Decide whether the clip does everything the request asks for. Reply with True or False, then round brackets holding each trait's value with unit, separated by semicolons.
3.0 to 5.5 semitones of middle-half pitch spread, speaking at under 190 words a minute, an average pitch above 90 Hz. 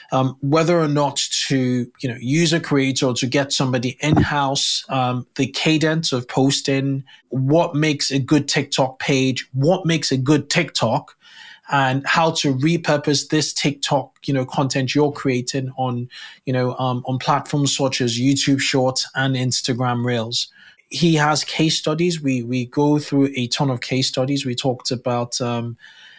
False (2.4 semitones; 165 wpm; 135 Hz)